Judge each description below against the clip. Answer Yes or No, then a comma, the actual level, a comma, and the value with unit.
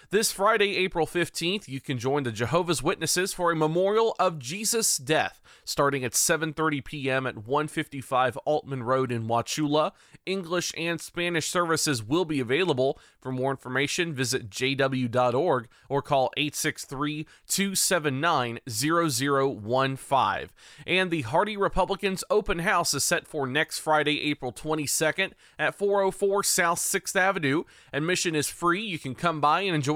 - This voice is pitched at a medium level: Yes, medium, 155 Hz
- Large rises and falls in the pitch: No, average, 4.7 semitones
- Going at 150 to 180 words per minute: No, slow, 135 wpm